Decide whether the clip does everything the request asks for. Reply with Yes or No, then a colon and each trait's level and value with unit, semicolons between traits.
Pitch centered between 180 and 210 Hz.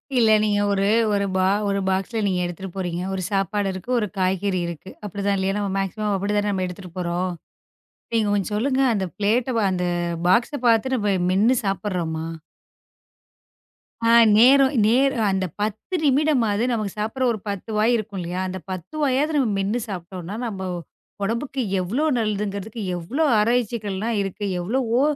Yes: high, 205 Hz